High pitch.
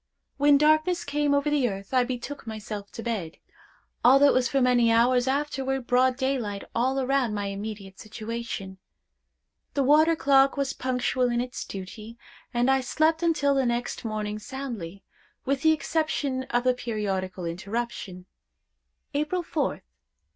Yes: very high, 250 Hz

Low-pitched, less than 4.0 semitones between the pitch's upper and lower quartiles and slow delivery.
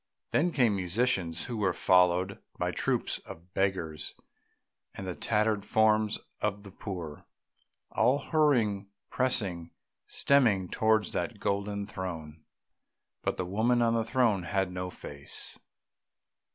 Yes: low, 100 Hz; average, 3.5 semitones; slow, 125 wpm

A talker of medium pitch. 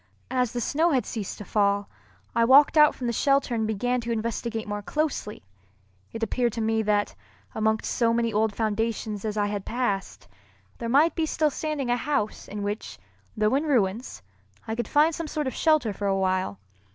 No: high, 230 Hz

